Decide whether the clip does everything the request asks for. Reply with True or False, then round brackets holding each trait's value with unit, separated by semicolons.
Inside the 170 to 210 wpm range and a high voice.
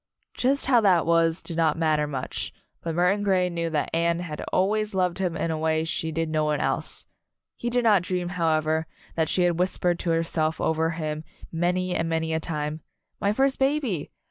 False (195 wpm; 170 Hz)